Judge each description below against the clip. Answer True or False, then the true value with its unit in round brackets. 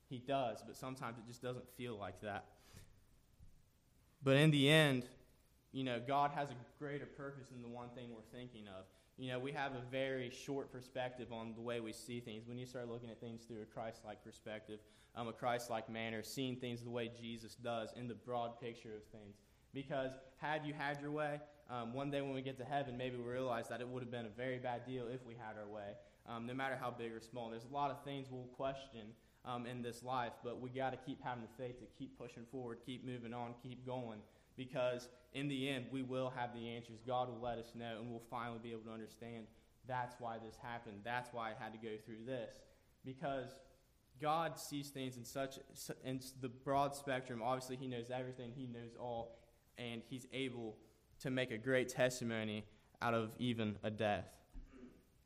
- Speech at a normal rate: False (215 wpm)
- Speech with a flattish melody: True (2.2 semitones)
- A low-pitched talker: True (125 Hz)